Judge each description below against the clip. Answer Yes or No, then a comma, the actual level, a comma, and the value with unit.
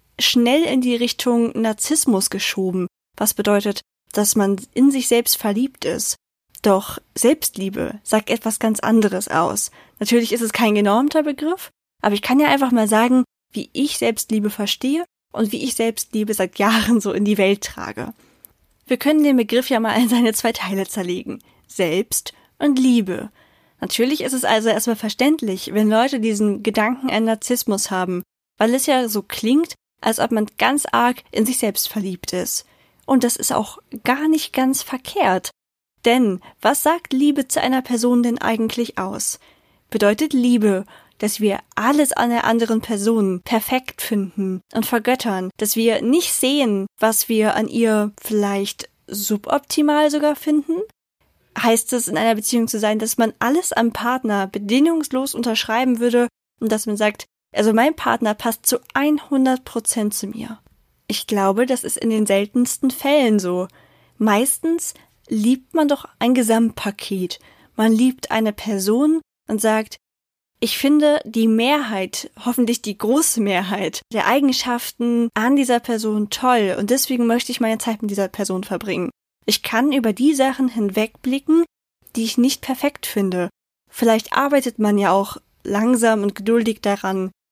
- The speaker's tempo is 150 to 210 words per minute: Yes, average, 155 wpm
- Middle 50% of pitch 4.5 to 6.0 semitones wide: No, average, 3.5 semitones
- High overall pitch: Yes, high, 230 Hz